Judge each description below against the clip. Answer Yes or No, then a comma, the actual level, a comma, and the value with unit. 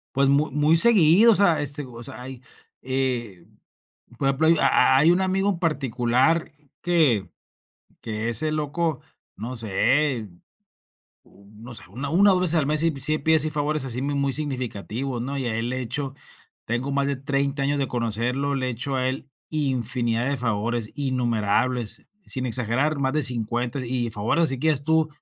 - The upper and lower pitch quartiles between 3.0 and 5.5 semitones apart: Yes, average, 4.1 semitones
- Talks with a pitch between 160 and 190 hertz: No, low, 135 Hz